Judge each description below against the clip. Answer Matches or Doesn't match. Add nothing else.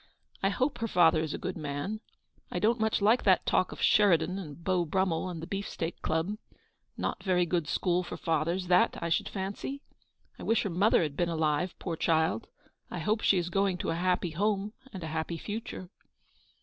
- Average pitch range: Matches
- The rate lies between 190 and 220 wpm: Matches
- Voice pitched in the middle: Matches